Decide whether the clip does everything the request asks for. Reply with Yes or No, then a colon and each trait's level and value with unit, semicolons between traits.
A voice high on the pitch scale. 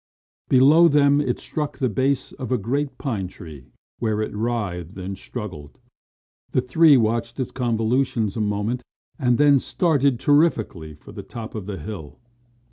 No: low, 120 Hz